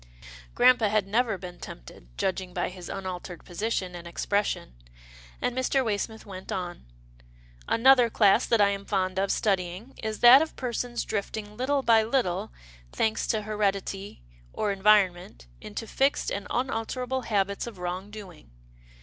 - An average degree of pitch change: Yes, average, 3.8 semitones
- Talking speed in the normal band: Yes, average, 150 wpm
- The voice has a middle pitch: No, high, 205 Hz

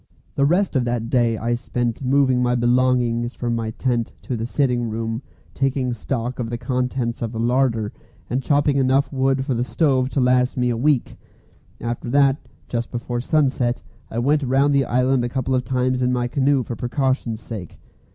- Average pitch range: No, narrow, 2.0 semitones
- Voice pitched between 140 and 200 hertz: No, low, 125 Hz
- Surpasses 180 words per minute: Yes, average, 190 wpm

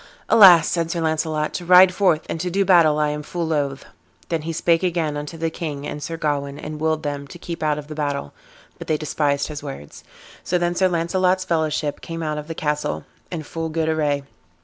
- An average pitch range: No, narrow, 2.3 semitones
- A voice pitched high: No, medium, 160 Hz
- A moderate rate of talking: No, fast, 215 wpm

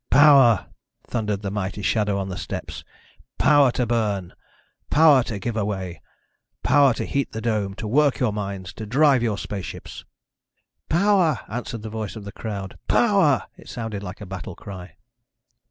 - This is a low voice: Yes, low, 110 Hz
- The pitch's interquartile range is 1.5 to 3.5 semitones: No, average, 4.9 semitones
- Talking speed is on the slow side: No, average, 160 wpm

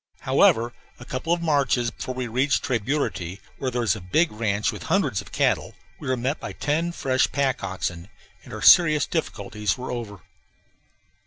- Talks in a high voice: No, low, 125 Hz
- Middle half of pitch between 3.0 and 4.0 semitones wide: No, average, 5.1 semitones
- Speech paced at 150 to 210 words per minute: Yes, average, 180 wpm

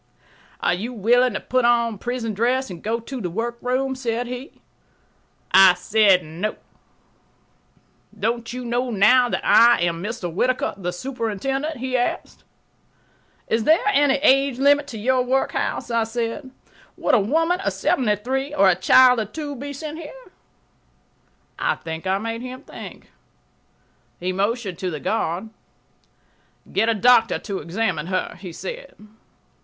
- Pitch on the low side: No, high, 235 Hz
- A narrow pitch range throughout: No, average, 4.4 semitones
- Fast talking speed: No, average, 150 wpm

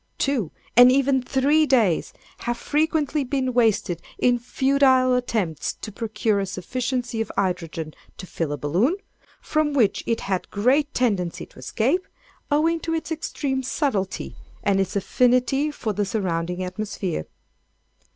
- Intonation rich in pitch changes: Yes, wide, 6.1 semitones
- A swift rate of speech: No, average, 140 wpm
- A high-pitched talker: Yes, high, 240 Hz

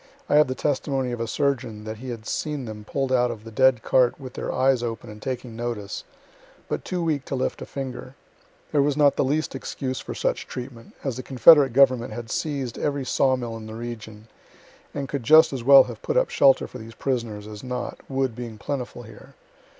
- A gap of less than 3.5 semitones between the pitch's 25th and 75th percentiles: Yes, average, 3.0 semitones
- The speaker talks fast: Yes, fast, 210 wpm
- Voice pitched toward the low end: Yes, low, 130 Hz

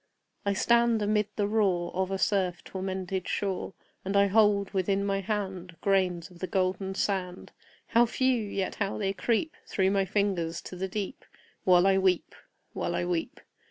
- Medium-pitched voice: No, high, 195 Hz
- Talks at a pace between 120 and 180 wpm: Yes, average, 170 wpm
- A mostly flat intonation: Yes, narrow, 1.8 semitones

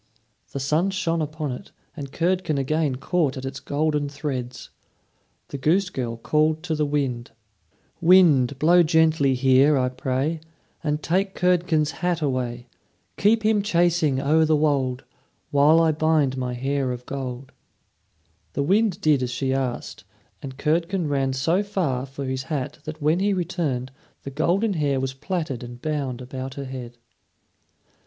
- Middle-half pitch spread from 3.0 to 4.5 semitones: Yes, average, 3.8 semitones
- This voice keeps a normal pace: Yes, average, 155 wpm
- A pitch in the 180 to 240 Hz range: No, medium, 145 Hz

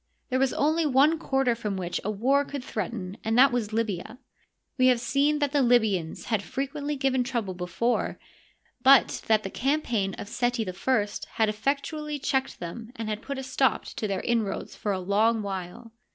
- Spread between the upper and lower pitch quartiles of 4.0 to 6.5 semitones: Yes, average, 4.5 semitones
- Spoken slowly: No, average, 180 wpm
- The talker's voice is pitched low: No, high, 235 Hz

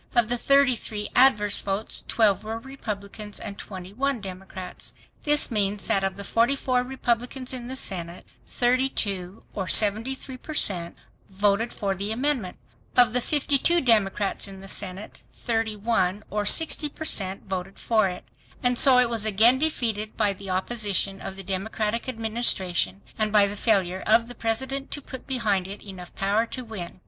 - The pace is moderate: Yes, average, 160 wpm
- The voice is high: Yes, high, 215 Hz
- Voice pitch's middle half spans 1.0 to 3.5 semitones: No, average, 4.0 semitones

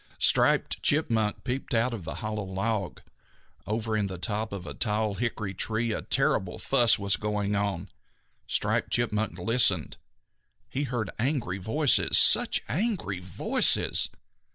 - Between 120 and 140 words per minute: Yes, slow, 135 wpm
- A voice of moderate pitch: No, low, 110 Hz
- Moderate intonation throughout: Yes, average, 3.1 semitones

